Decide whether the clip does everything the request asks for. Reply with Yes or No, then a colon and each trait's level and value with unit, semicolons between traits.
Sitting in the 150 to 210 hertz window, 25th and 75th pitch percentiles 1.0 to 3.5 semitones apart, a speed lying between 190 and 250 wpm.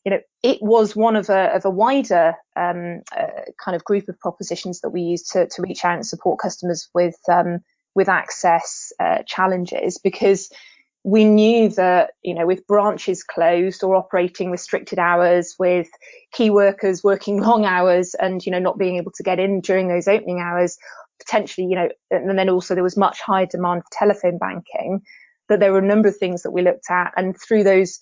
Yes: high, 190 Hz; narrow, 2.6 semitones; average, 200 wpm